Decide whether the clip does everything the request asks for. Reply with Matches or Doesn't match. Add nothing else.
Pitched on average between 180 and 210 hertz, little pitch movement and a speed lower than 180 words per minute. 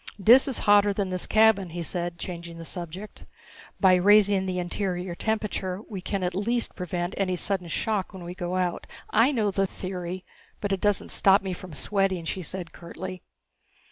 Doesn't match